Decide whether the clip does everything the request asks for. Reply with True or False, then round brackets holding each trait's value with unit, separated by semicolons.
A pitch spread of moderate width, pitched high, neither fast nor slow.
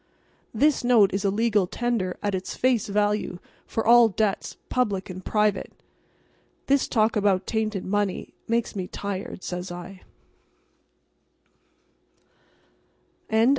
False (3.1 semitones; 205 Hz; 115 wpm)